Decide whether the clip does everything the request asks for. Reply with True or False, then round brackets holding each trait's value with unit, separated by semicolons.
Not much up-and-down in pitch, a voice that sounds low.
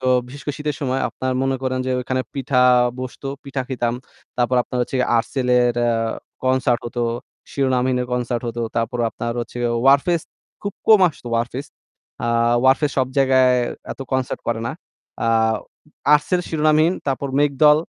True (2.2 semitones; 130 Hz)